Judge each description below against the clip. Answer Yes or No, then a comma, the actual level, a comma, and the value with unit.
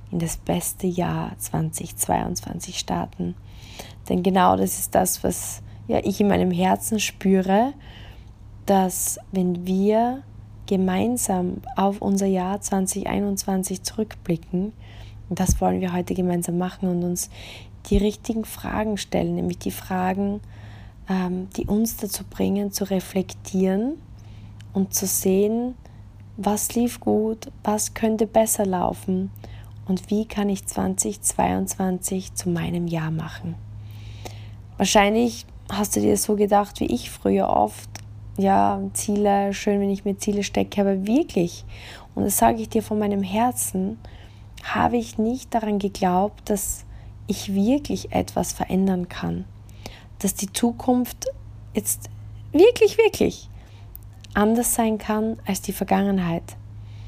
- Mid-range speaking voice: Yes, medium, 180 Hz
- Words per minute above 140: No, slow, 125 wpm